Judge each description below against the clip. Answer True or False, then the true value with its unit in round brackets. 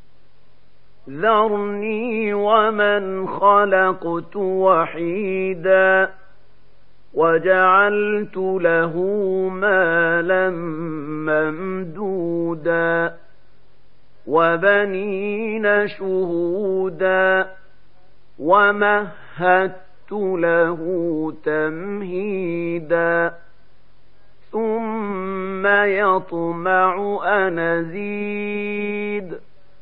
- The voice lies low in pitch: False (190 Hz)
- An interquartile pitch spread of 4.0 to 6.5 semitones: False (3.2 semitones)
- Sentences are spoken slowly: True (30 wpm)